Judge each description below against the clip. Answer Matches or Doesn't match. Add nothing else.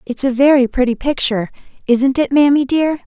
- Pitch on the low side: Doesn't match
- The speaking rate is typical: Matches